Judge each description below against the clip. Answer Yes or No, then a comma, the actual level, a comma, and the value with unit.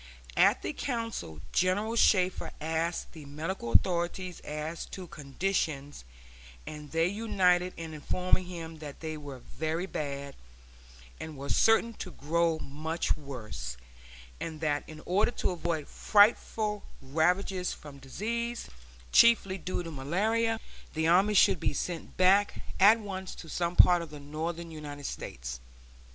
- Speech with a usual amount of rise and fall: Yes, average, 4.0 semitones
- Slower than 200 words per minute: Yes, average, 140 wpm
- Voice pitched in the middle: Yes, medium, 170 Hz